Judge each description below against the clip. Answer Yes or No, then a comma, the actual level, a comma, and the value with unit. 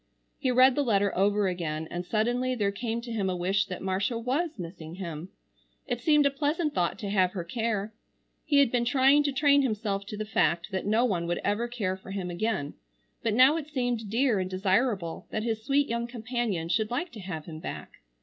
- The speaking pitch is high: Yes, high, 215 Hz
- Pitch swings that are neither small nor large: Yes, average, 5.0 semitones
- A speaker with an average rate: No, fast, 215 wpm